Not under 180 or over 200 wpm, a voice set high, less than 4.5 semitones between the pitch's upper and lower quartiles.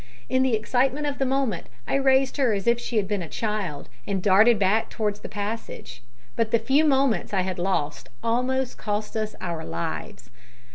No: average, 190 wpm; high, 220 Hz; average, 5.0 semitones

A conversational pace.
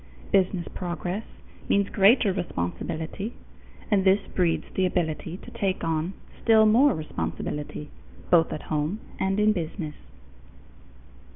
No: slow, 115 wpm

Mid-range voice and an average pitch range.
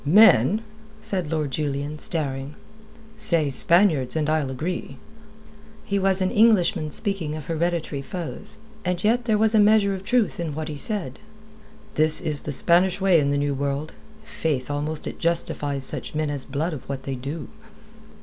Yes: medium, 155 Hz; average, 4.6 semitones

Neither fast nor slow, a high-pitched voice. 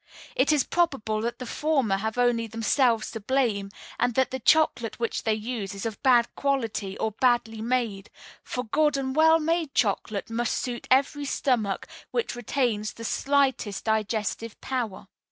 Yes: average, 160 wpm; high, 240 Hz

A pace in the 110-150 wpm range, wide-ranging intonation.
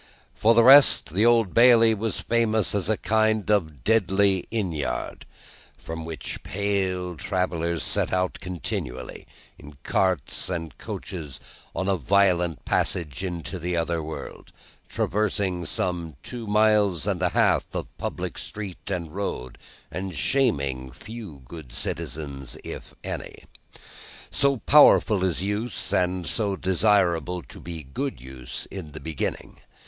No: slow, 135 wpm; average, 4.7 semitones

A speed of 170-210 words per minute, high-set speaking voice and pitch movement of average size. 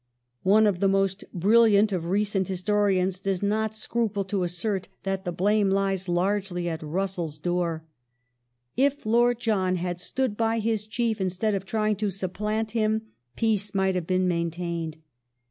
Yes: average, 175 wpm; high, 195 Hz; average, 3.1 semitones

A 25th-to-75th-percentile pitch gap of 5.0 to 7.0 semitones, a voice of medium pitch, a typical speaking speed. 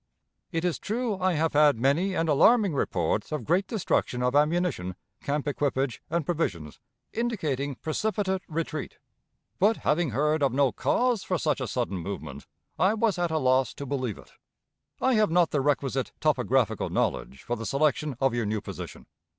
Yes: wide, 5.6 semitones; medium, 150 Hz; average, 170 wpm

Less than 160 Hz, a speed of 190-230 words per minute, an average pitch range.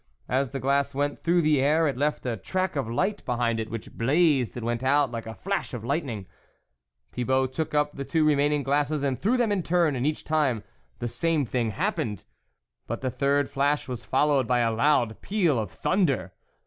Yes: medium, 140 Hz; average, 200 wpm; average, 3.8 semitones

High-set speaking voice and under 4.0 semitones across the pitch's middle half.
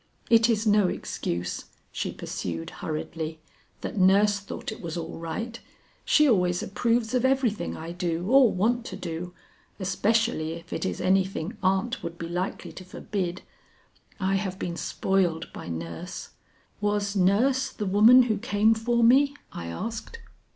No: high, 195 Hz; average, 4.8 semitones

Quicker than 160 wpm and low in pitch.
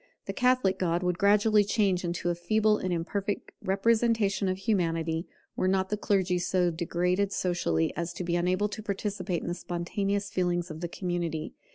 No: average, 175 wpm; medium, 185 Hz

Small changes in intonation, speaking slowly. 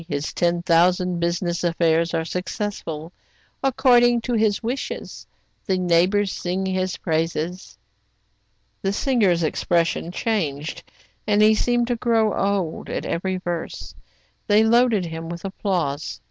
No: average, 4.0 semitones; slow, 125 wpm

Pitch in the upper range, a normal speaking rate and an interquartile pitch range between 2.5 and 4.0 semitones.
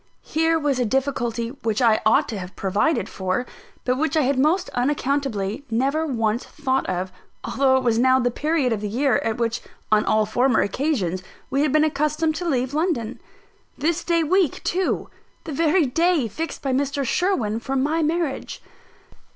No: very high, 270 Hz; average, 175 wpm; average, 5.0 semitones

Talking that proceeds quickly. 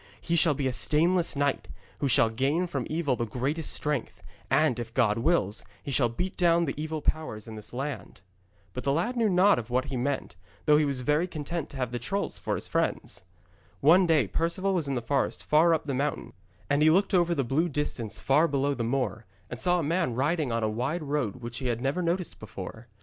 Yes: fast, 225 wpm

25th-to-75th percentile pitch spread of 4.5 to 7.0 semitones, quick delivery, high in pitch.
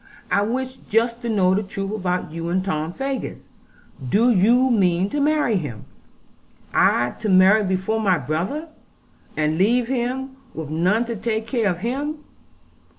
No: average, 5.0 semitones; average, 155 wpm; high, 210 Hz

